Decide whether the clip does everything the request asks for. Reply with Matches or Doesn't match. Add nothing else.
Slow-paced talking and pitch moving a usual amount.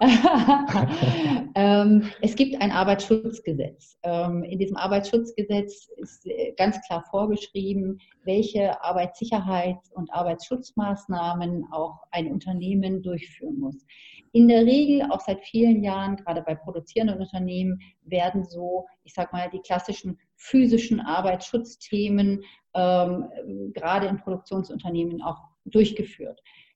Matches